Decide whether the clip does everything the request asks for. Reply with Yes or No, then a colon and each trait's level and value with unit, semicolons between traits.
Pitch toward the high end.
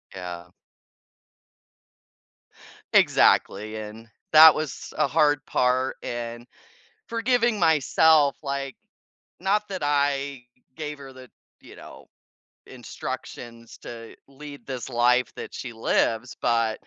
No: low, 135 Hz